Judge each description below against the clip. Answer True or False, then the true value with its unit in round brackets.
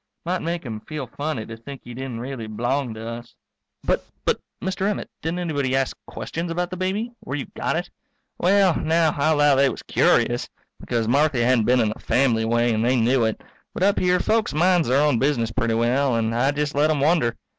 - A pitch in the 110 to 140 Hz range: True (135 Hz)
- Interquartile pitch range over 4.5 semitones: True (5.5 semitones)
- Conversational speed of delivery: False (215 wpm)